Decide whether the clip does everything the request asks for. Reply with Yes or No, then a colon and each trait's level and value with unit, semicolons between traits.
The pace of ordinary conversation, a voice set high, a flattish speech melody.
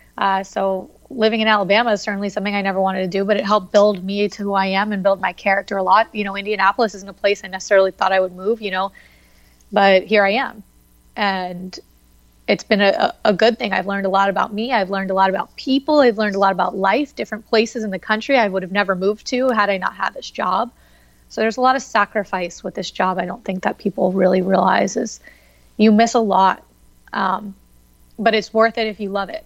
No: fast, 240 wpm; high, 200 Hz; narrow, 2.2 semitones